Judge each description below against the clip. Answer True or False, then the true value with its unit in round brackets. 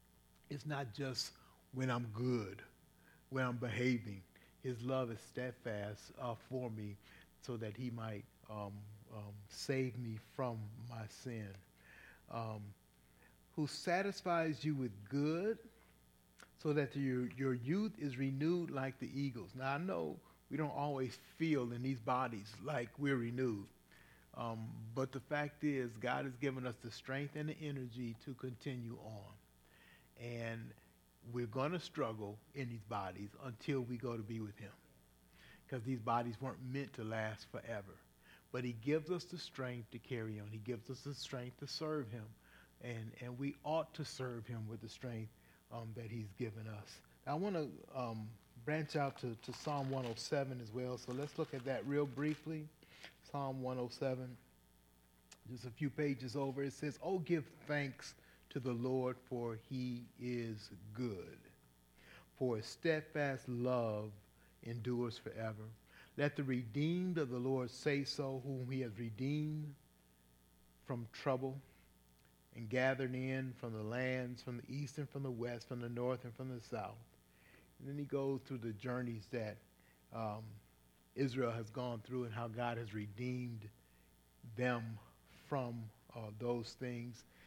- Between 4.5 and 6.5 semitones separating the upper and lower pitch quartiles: False (3.7 semitones)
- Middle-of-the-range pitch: False (125 Hz)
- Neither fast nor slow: True (155 wpm)